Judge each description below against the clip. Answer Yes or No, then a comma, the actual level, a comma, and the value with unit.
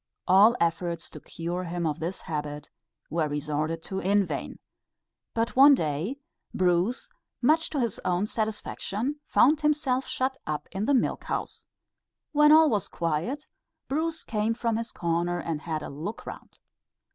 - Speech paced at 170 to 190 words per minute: No, average, 155 wpm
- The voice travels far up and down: Yes, wide, 7.6 semitones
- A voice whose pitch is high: Yes, high, 195 Hz